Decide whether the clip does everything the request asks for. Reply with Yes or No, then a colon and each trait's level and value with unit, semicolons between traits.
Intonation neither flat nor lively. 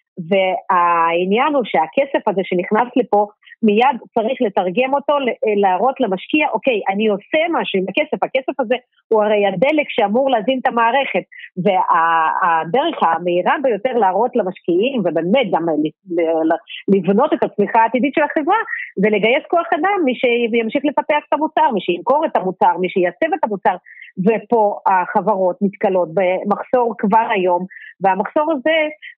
No: wide, 6.6 semitones